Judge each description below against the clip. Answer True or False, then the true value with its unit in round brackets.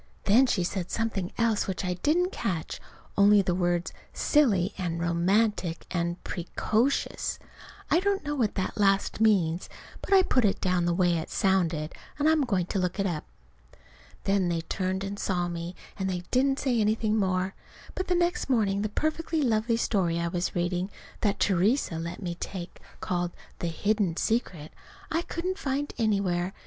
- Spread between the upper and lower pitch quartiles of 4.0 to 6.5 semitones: True (4.6 semitones)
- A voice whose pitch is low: False (195 Hz)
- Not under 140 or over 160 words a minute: False (175 wpm)